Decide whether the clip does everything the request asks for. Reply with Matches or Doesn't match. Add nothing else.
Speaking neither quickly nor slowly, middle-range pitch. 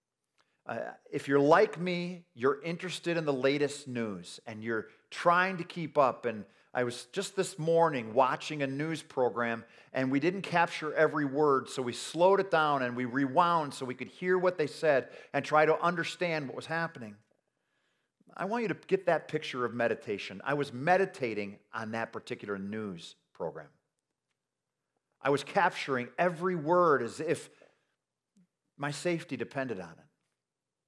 Matches